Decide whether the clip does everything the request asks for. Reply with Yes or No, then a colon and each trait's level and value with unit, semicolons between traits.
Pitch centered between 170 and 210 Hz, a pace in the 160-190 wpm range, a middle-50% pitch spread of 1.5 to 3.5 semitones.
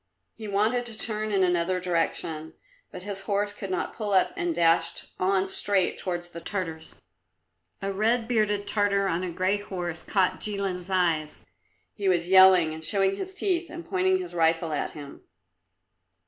Yes: high, 190 Hz; average, 165 wpm; average, 3.1 semitones